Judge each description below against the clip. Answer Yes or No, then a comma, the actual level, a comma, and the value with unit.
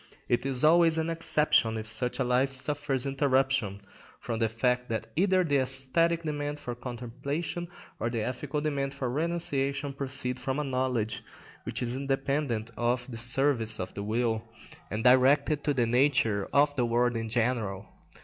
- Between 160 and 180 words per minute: Yes, average, 165 wpm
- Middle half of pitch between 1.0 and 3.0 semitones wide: No, average, 3.4 semitones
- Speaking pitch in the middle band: No, low, 130 Hz